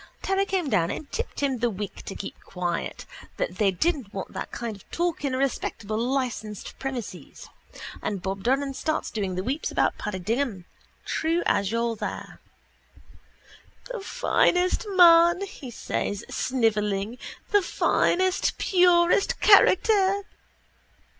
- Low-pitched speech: No, very high, 260 Hz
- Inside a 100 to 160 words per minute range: Yes, slow, 135 wpm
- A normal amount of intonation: No, wide, 8.9 semitones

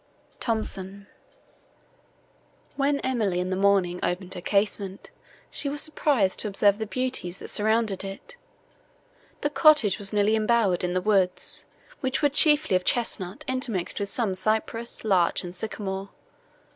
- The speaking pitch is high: Yes, high, 205 Hz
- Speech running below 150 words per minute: Yes, average, 140 wpm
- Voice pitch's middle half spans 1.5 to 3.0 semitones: No, average, 4.2 semitones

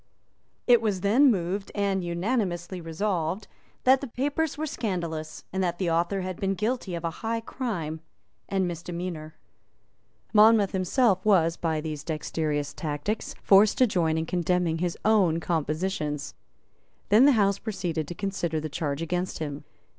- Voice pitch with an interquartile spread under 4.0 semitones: No, average, 4.3 semitones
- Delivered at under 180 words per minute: Yes, average, 150 wpm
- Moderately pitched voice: Yes, medium, 180 Hz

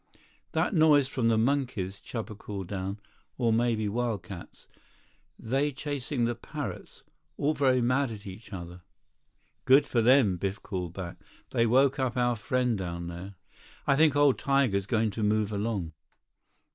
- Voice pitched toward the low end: Yes, low, 115 Hz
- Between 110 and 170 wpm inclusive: Yes, average, 155 wpm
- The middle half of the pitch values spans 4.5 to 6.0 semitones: Yes, average, 4.9 semitones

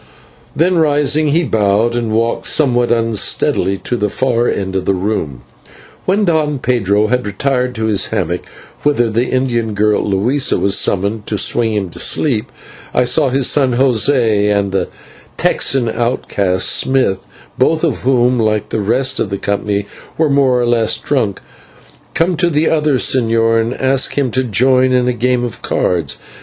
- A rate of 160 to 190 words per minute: Yes, average, 165 wpm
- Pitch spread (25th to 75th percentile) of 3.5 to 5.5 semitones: Yes, average, 4.0 semitones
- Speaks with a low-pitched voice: Yes, low, 120 Hz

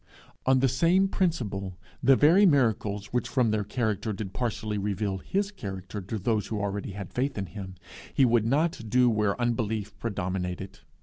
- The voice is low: Yes, low, 110 Hz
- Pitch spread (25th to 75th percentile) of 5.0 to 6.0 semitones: No, average, 4.3 semitones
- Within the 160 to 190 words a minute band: Yes, average, 170 wpm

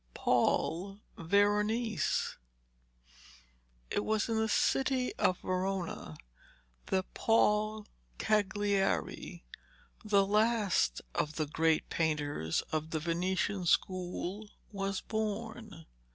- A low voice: No, high, 195 Hz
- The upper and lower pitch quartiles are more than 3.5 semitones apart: Yes, average, 3.9 semitones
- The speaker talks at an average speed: No, slow, 90 wpm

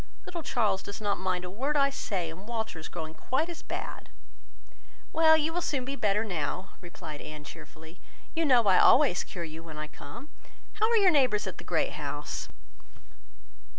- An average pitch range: No, wide, 9.0 semitones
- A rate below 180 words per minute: No, average, 185 wpm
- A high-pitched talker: Yes, high, 205 Hz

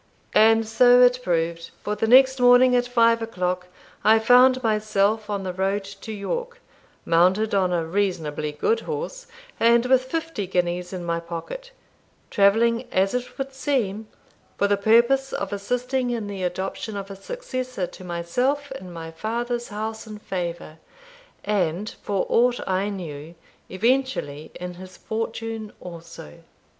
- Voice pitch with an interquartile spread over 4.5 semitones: Yes, average, 5.2 semitones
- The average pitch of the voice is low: No, high, 210 Hz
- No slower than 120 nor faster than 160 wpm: Yes, average, 150 wpm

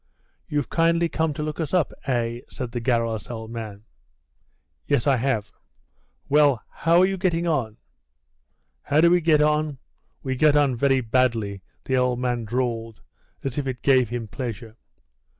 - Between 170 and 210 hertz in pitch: No, low, 130 Hz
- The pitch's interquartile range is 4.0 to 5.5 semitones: Yes, average, 4.5 semitones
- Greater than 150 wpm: Yes, average, 165 wpm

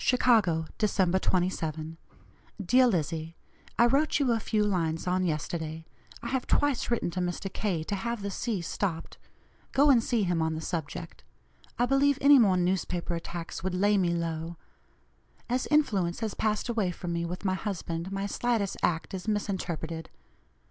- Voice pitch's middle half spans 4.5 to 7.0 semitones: Yes, average, 5.1 semitones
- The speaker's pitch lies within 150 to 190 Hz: Yes, medium, 185 Hz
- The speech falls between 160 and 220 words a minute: Yes, average, 165 wpm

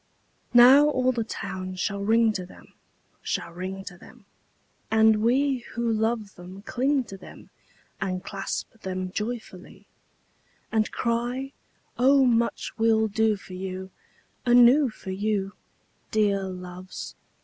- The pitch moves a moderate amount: Yes, average, 4.1 semitones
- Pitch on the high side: Yes, high, 220 Hz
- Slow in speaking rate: Yes, slow, 130 wpm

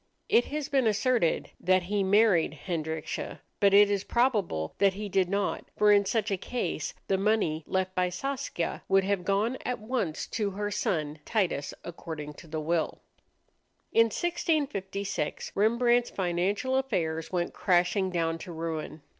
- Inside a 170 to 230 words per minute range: No, average, 155 wpm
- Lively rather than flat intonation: No, average, 4.3 semitones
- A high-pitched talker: Yes, high, 195 Hz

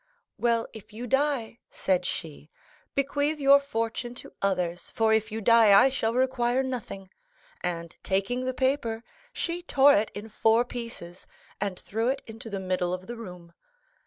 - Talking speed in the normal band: Yes, average, 165 wpm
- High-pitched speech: Yes, high, 225 Hz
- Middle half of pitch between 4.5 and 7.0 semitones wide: Yes, average, 4.9 semitones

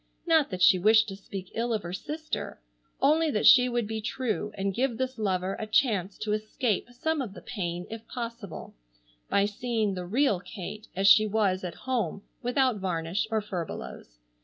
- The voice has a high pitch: Yes, high, 215 Hz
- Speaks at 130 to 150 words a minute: No, average, 185 wpm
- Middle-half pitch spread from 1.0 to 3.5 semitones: No, average, 4.1 semitones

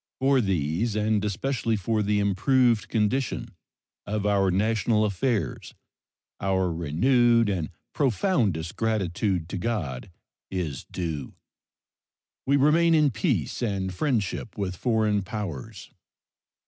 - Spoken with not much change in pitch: No, average, 4.2 semitones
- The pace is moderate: No, slow, 110 wpm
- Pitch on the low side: Yes, low, 105 Hz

